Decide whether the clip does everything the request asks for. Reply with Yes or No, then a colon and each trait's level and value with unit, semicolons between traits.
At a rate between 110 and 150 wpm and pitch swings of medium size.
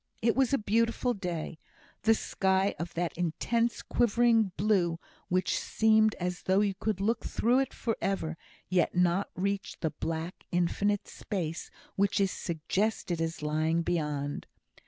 Yes: average, 145 wpm; average, 4.4 semitones